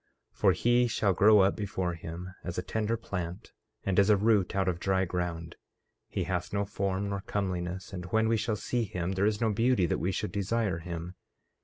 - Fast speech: Yes, fast, 210 wpm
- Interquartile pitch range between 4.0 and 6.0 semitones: No, average, 2.9 semitones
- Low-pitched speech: Yes, very low, 95 Hz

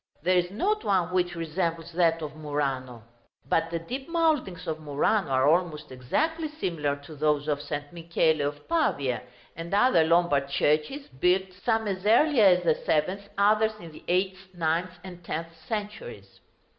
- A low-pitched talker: No, medium, 170 Hz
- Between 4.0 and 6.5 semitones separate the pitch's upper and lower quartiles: Yes, average, 4.7 semitones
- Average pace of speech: Yes, average, 160 wpm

